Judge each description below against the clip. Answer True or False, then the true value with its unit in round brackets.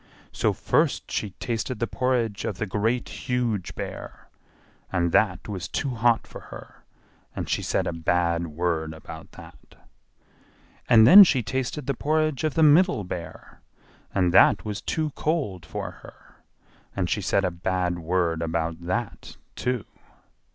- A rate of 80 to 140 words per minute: False (150 wpm)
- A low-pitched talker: True (105 Hz)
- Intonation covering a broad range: True (6.3 semitones)